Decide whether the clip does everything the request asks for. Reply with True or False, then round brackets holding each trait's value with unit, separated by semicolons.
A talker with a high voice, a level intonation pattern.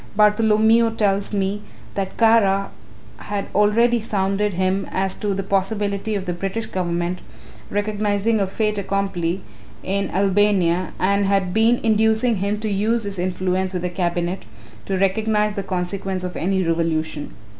True (195 Hz; 2.1 semitones)